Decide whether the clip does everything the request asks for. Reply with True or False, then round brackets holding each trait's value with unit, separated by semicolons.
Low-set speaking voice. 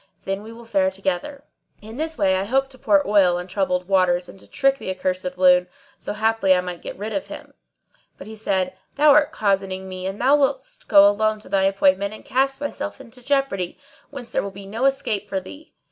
False (200 Hz)